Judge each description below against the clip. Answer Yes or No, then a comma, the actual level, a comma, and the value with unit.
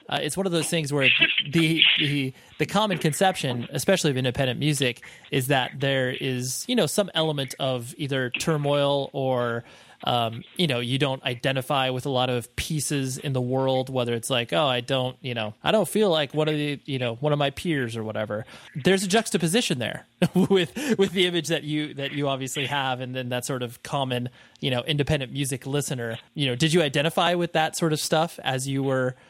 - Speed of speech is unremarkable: No, fast, 210 wpm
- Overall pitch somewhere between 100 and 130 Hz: No, medium, 140 Hz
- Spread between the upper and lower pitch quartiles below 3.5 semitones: No, average, 3.8 semitones